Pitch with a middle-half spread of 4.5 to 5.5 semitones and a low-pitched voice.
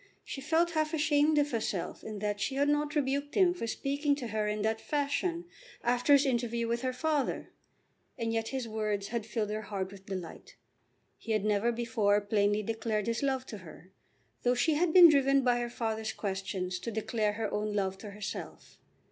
No: average, 5.0 semitones; high, 230 Hz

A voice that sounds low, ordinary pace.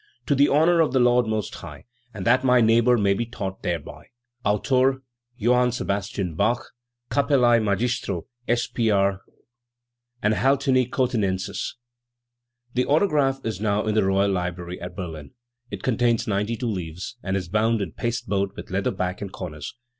Yes: low, 110 Hz; average, 165 wpm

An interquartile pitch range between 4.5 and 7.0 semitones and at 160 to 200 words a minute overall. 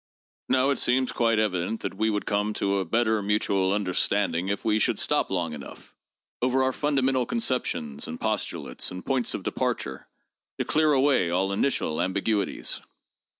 Yes: average, 5.3 semitones; average, 165 wpm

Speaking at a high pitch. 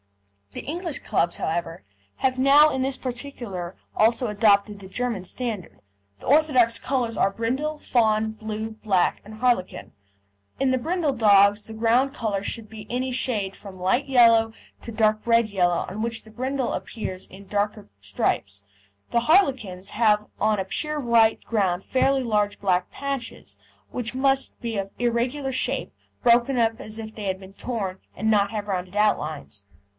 Yes: high, 220 Hz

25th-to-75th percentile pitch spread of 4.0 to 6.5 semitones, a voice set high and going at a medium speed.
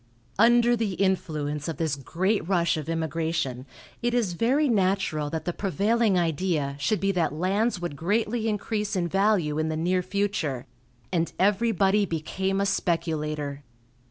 No: average, 4.5 semitones; medium, 180 Hz; average, 150 wpm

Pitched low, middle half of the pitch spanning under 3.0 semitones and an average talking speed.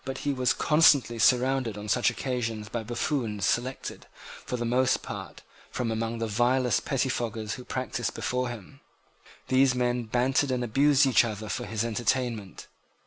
Yes: low, 120 Hz; narrow, 2.4 semitones; average, 150 wpm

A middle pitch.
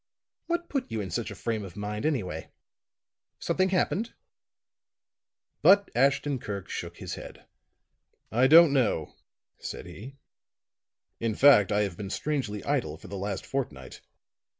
No: low, 115 Hz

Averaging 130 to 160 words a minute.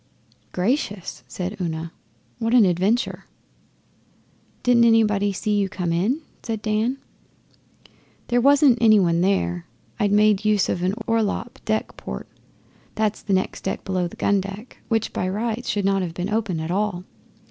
Yes: average, 155 wpm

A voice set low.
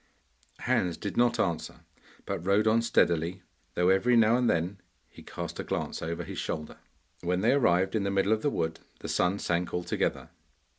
Yes: very low, 95 Hz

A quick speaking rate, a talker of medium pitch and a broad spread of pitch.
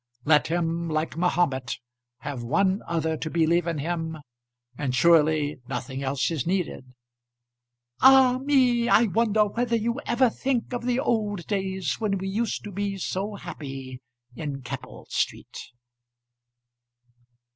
No: slow, 135 wpm; medium, 175 Hz; wide, 6.3 semitones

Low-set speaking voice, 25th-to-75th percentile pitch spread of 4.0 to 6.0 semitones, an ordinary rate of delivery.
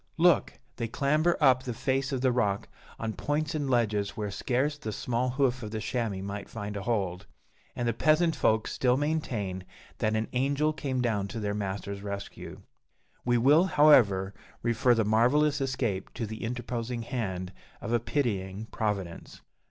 Yes: low, 120 Hz; average, 4.6 semitones; average, 165 wpm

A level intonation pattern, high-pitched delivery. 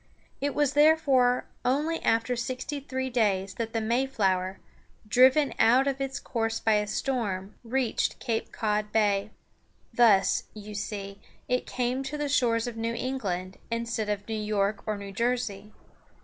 No: average, 3.8 semitones; high, 230 Hz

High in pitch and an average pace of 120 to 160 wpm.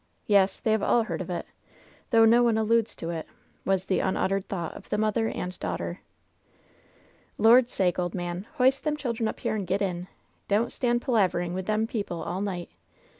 No: high, 205 Hz; average, 190 wpm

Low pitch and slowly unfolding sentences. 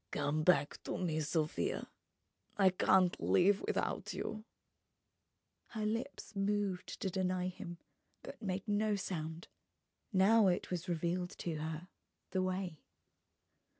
No: medium, 185 Hz; slow, 125 wpm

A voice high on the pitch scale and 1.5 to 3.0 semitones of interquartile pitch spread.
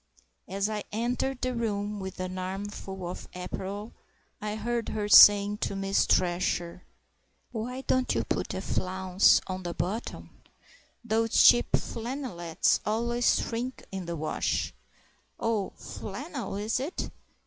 No: high, 205 Hz; average, 3.8 semitones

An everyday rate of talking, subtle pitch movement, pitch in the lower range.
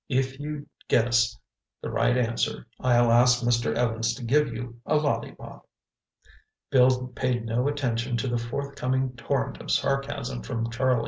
Yes: average, 150 wpm; narrow, 2.2 semitones; low, 125 Hz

